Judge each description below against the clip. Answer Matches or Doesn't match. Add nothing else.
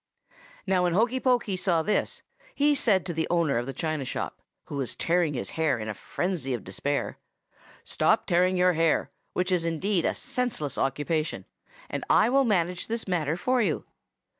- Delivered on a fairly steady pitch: Doesn't match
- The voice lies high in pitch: Doesn't match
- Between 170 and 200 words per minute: Matches